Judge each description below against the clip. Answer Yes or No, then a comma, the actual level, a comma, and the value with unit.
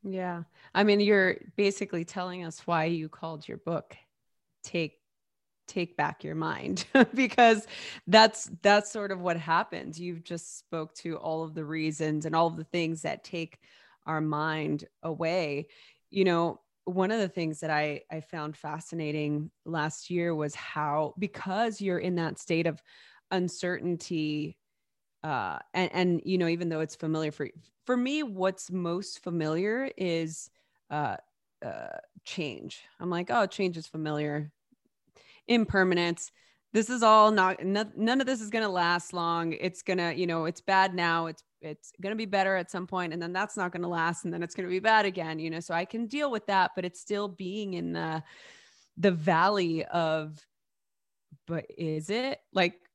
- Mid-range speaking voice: Yes, medium, 175 Hz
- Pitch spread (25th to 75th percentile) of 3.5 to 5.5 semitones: No, average, 3.1 semitones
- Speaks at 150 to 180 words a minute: Yes, average, 170 wpm